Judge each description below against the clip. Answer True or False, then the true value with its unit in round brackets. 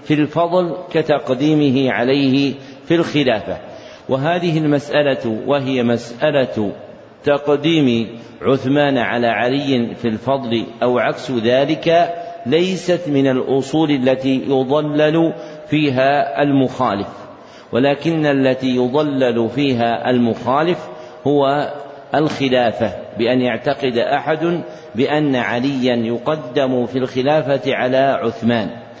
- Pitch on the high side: False (135 Hz)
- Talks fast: False (90 wpm)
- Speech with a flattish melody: False (3.1 semitones)